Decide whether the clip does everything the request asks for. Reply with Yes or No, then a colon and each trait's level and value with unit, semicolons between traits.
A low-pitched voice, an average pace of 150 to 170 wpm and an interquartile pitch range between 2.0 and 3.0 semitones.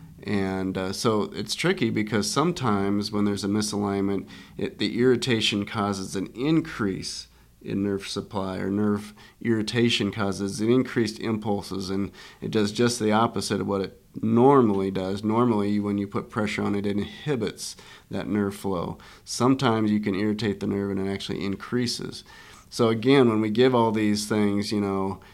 Yes: low, 105 Hz; average, 165 wpm; narrow, 2.4 semitones